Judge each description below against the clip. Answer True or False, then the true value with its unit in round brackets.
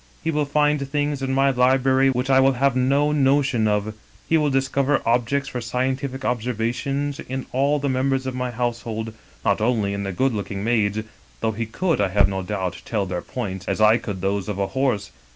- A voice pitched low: True (125 Hz)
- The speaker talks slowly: False (205 wpm)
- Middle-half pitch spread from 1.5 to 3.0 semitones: False (4.2 semitones)